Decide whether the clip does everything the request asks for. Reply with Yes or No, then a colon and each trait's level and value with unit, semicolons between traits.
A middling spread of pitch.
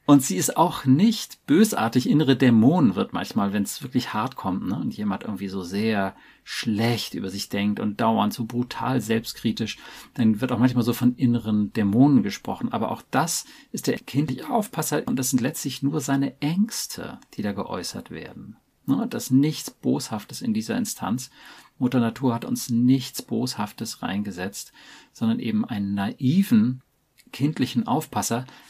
Yes: average, 4.7 semitones